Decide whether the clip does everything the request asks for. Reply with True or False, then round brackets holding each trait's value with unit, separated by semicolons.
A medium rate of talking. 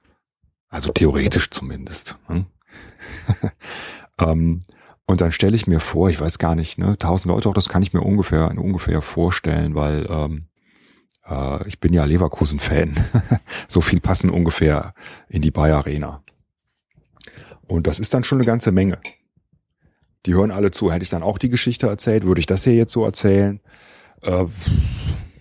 True (155 wpm)